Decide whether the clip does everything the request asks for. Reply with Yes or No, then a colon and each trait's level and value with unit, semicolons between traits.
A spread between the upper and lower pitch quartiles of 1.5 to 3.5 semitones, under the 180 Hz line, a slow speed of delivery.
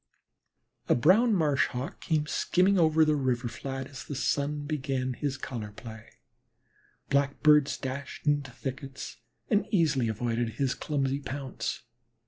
Yes: narrow, 2.6 semitones; medium, 140 Hz; slow, 130 wpm